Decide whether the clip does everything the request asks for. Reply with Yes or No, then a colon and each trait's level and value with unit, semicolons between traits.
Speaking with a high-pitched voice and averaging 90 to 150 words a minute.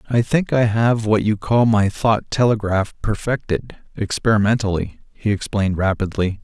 No: low, 105 Hz; average, 140 wpm